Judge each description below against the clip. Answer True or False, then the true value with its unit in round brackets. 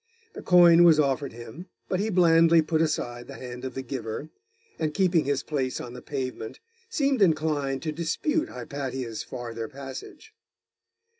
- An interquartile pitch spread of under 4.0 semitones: False (4.6 semitones)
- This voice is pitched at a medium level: True (145 Hz)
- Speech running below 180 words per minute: True (155 wpm)